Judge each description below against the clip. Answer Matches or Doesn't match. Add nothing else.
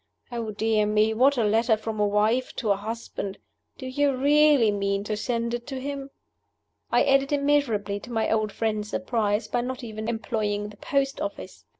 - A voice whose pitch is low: Doesn't match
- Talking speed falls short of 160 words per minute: Doesn't match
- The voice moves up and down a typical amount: Matches